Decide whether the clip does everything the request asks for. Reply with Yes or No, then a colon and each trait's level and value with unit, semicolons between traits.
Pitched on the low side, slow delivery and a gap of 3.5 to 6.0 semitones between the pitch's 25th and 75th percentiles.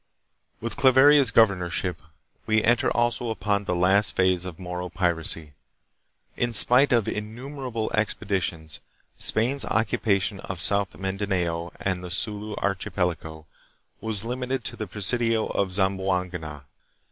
Yes: low, 100 Hz; slow, 125 wpm; average, 4.0 semitones